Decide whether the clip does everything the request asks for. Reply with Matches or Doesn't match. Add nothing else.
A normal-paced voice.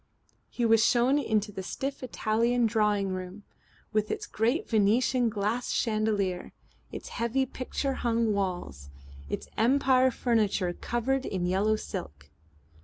Doesn't match